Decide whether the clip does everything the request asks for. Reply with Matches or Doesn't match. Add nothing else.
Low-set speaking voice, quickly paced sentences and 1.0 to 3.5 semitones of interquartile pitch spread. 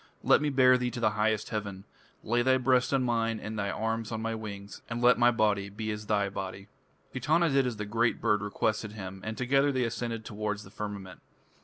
Matches